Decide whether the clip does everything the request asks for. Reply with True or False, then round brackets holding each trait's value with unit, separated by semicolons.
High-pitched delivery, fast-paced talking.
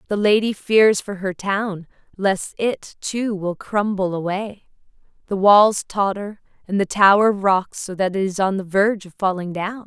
False (200 Hz; 175 wpm)